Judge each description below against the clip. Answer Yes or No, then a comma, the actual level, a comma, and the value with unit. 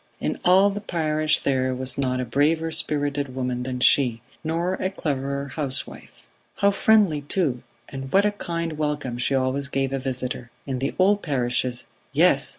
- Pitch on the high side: No, medium, 140 Hz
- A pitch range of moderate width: Yes, average, 4.1 semitones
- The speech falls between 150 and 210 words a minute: Yes, average, 165 wpm